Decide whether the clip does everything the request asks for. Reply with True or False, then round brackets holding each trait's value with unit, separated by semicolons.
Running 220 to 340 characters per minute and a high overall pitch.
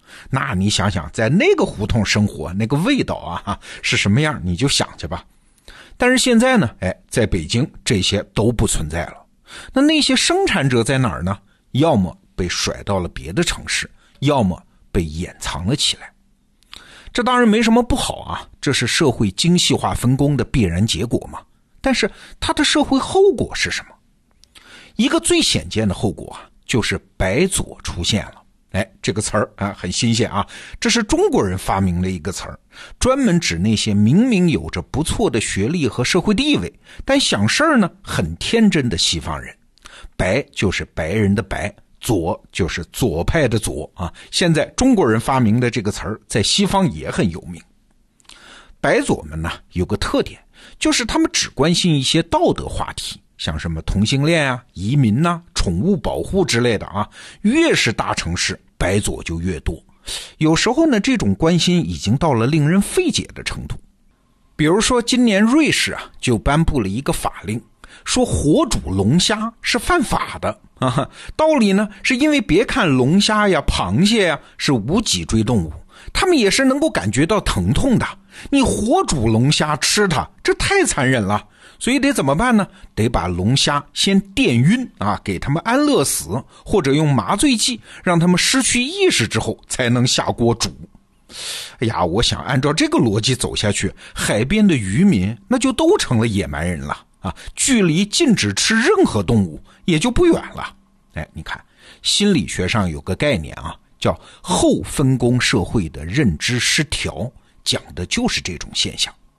False (250 characters per minute; 135 Hz)